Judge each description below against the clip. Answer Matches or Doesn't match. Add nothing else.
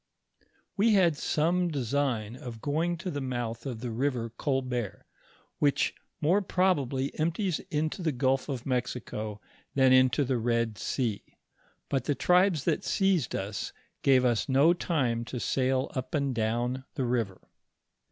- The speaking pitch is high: Doesn't match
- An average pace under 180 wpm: Matches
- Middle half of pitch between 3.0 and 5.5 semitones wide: Matches